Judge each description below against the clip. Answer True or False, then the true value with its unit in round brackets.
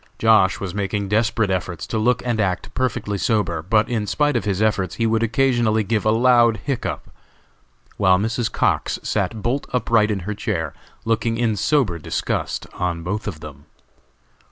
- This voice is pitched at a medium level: False (110 Hz)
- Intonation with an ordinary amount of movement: True (3.2 semitones)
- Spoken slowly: False (170 wpm)